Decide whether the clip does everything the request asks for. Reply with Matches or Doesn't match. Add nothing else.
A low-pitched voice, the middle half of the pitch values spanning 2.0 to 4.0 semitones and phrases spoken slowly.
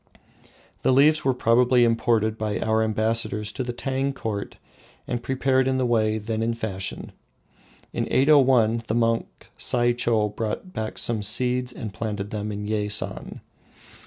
Doesn't match